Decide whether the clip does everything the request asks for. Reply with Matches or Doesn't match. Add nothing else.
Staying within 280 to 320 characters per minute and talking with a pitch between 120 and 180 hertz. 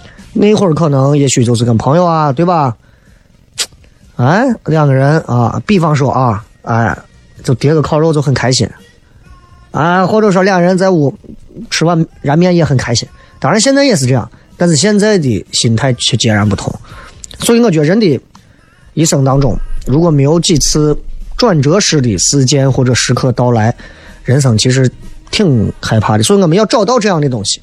Doesn't match